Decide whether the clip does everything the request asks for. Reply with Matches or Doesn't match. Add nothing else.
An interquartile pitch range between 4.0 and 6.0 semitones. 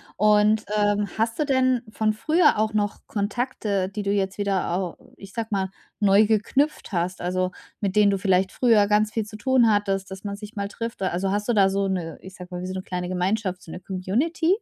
Doesn't match